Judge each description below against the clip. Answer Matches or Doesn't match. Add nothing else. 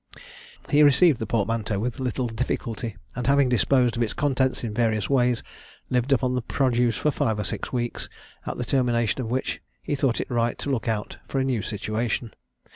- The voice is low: Matches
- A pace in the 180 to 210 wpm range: Matches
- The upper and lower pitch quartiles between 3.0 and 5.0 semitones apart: Doesn't match